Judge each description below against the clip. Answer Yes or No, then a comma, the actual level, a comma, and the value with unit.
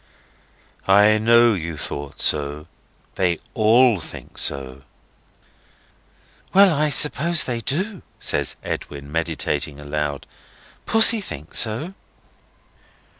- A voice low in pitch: Yes, low, 105 Hz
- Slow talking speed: Yes, slow, 95 wpm